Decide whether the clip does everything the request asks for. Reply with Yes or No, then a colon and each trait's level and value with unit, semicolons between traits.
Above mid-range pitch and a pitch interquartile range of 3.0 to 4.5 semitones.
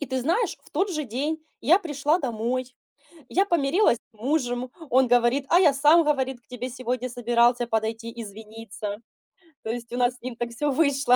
Yes: very high, 255 Hz; average, 3.6 semitones